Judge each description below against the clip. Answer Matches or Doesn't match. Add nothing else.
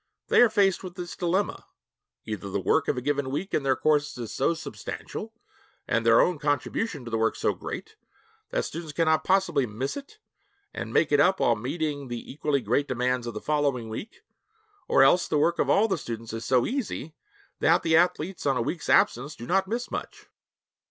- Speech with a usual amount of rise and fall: Doesn't match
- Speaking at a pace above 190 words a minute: Matches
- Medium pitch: Matches